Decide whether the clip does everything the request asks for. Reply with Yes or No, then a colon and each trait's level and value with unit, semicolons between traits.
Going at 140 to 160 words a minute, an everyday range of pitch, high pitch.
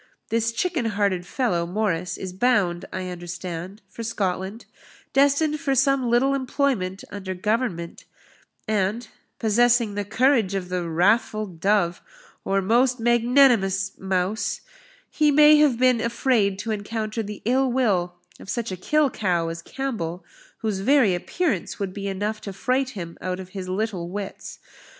Yes: average, 145 wpm; average, 4.7 semitones; high, 210 Hz